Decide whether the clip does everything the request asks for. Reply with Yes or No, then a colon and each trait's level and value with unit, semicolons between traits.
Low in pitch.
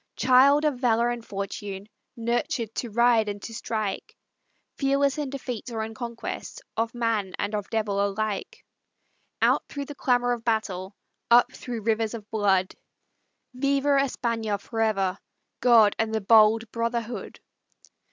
No: high, 225 Hz